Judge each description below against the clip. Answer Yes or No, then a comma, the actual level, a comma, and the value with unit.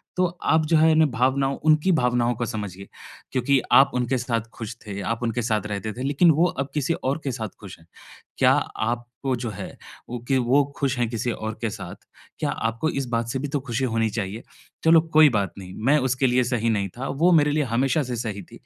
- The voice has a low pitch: Yes, low, 125 Hz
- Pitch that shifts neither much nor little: Yes, average, 3.7 semitones